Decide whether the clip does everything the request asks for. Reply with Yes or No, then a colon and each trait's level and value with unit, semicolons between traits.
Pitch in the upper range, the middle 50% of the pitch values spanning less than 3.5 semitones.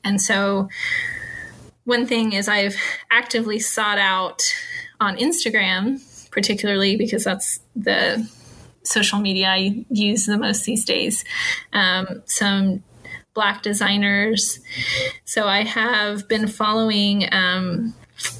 Yes: high, 215 Hz; narrow, 2.6 semitones